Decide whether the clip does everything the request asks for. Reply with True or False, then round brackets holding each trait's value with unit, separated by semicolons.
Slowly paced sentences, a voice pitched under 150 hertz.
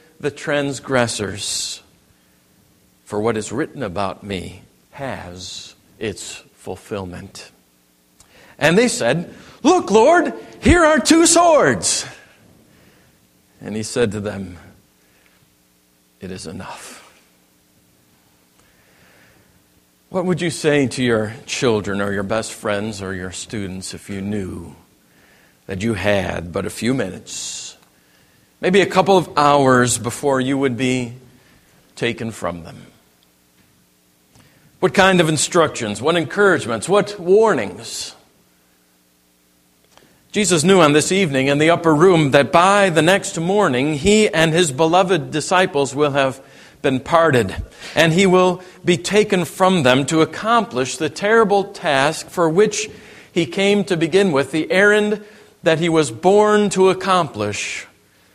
True (125 wpm; 140 Hz)